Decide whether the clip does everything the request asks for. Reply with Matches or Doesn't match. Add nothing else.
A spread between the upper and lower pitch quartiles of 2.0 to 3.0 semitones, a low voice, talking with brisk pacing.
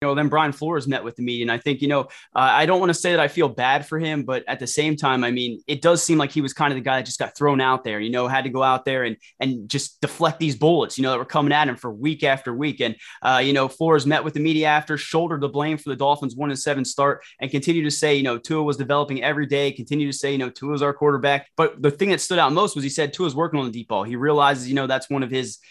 Doesn't match